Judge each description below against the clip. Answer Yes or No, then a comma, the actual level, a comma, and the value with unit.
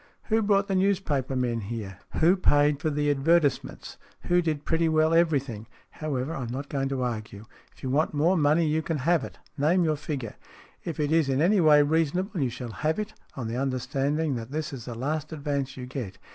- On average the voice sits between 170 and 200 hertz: No, medium, 145 Hz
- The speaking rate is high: Yes, fast, 210 wpm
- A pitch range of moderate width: Yes, average, 3.8 semitones